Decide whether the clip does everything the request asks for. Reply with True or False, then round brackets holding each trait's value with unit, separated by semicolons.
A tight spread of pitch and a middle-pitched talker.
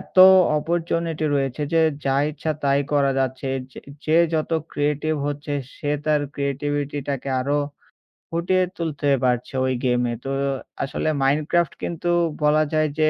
True (2.2 semitones; 145 Hz)